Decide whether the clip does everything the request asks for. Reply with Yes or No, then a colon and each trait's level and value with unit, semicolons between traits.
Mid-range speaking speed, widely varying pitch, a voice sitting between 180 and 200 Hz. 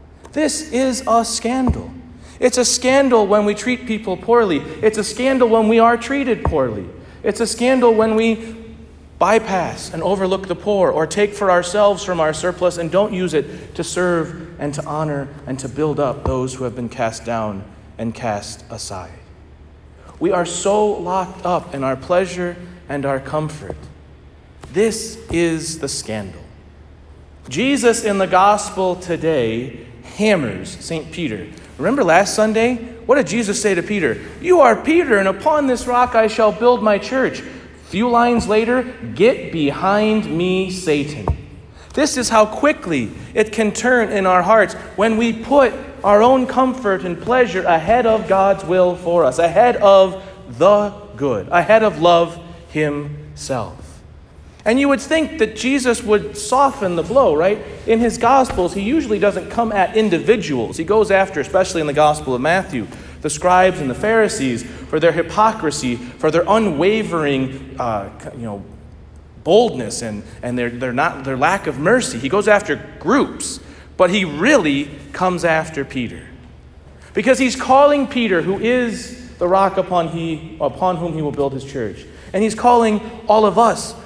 Yes: average, 165 wpm; wide, 7.2 semitones; high, 190 Hz